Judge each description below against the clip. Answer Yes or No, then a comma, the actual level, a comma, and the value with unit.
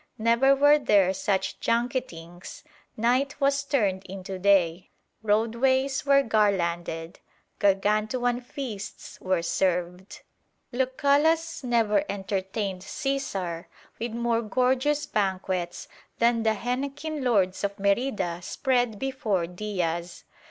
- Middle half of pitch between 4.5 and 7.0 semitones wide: Yes, wide, 5.6 semitones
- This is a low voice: No, high, 215 Hz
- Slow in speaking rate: Yes, slow, 100 wpm